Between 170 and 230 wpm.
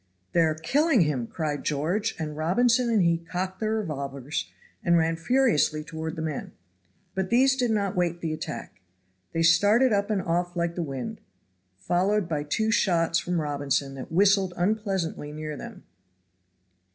No: average, 160 wpm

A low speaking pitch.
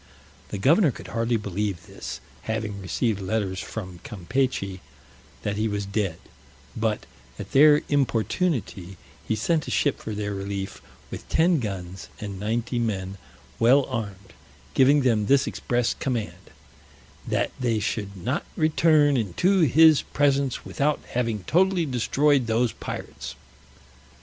Yes: low, 115 Hz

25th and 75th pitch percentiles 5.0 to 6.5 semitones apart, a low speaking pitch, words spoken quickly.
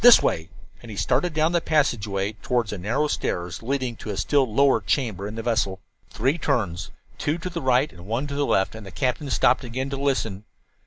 Yes: wide, 5.5 semitones; low, 125 Hz; fast, 215 wpm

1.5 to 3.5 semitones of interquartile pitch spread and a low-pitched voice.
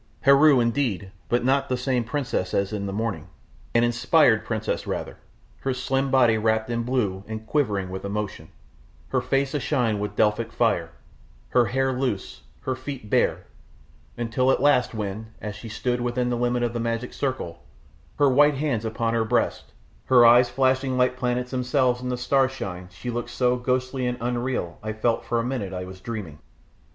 Yes: average, 2.9 semitones; low, 120 Hz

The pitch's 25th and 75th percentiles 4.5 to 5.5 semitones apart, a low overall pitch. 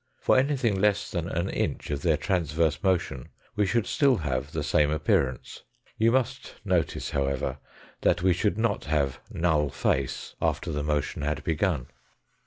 Yes: average, 5.2 semitones; very low, 80 Hz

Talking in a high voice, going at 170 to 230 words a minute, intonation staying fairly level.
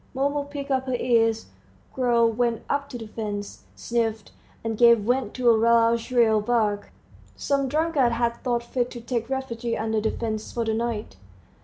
Yes: high, 235 Hz; average, 175 wpm; narrow, 2.2 semitones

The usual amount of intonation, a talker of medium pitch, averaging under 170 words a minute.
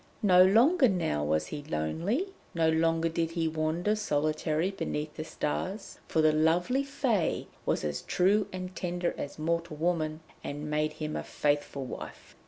Yes: average, 3.3 semitones; medium, 165 Hz; average, 160 wpm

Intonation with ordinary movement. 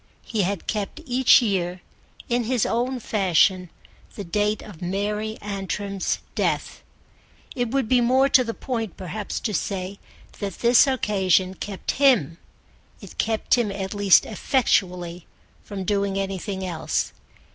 Yes: average, 3.7 semitones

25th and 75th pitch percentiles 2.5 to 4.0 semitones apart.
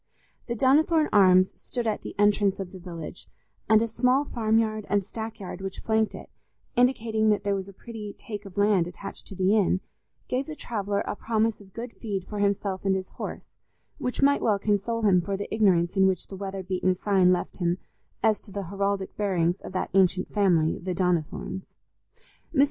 Yes: average, 2.8 semitones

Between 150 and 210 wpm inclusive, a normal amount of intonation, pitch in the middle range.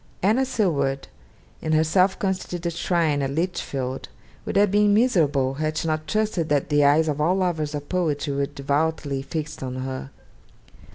Yes: average, 165 wpm; average, 4.4 semitones; medium, 155 Hz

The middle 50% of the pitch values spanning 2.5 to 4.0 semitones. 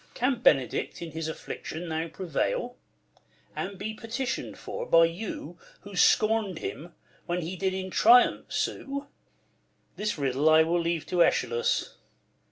No: average, 5.1 semitones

